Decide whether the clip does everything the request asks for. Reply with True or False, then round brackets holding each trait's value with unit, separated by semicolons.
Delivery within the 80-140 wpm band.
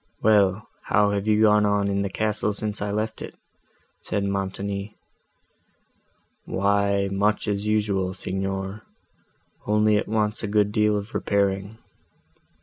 True (135 wpm)